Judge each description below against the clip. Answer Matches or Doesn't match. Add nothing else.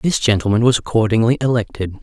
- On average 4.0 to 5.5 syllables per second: Doesn't match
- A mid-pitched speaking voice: Doesn't match